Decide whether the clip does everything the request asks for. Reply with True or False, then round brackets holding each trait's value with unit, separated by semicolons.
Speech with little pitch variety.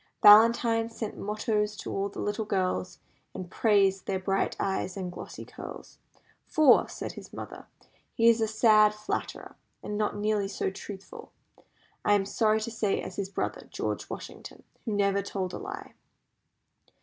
True (2.0 semitones)